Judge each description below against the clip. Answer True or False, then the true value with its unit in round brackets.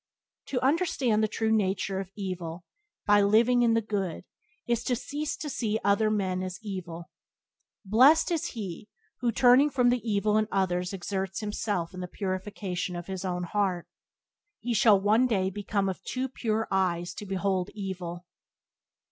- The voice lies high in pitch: True (205 Hz)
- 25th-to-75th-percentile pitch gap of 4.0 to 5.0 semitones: False (3.5 semitones)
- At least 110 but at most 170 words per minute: True (165 wpm)